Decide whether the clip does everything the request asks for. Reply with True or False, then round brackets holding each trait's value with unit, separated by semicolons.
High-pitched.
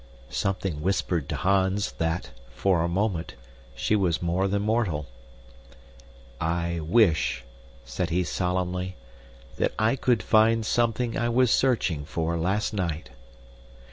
False (95 Hz)